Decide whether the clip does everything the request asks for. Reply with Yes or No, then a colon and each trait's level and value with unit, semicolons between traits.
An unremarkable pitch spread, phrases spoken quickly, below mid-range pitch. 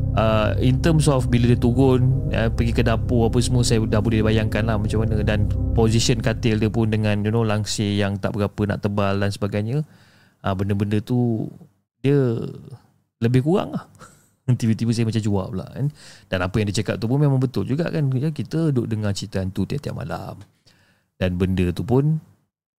Yes: average, 3.5 semitones; fast, 185 wpm; low, 110 Hz